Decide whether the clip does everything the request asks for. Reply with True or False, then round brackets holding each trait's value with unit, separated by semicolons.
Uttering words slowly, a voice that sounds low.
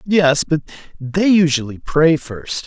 False (115 wpm; 155 Hz)